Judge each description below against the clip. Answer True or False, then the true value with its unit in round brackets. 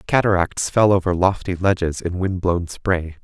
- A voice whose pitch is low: True (90 Hz)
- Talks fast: False (165 wpm)